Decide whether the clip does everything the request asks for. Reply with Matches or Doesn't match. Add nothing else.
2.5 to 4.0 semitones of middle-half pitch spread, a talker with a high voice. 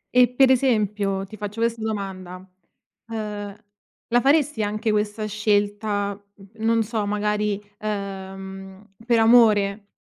Doesn't match